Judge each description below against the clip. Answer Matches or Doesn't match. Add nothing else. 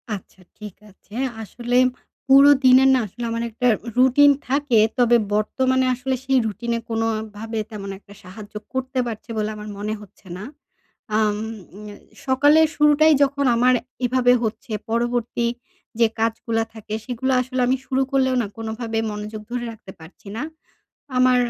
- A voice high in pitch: Matches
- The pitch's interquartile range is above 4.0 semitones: Doesn't match